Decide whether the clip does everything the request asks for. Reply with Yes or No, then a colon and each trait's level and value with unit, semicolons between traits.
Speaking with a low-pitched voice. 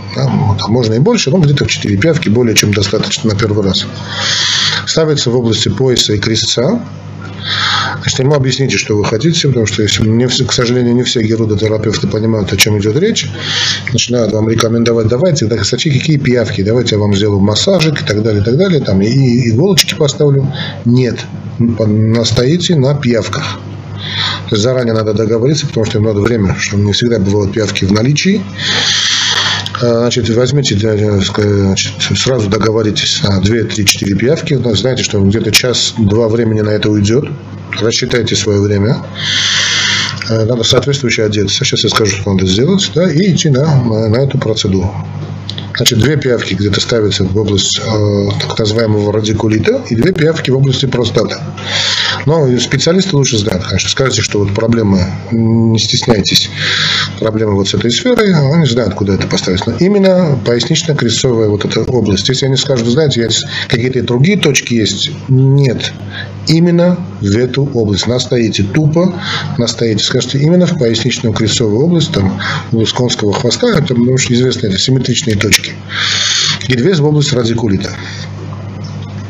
Yes: low, 115 Hz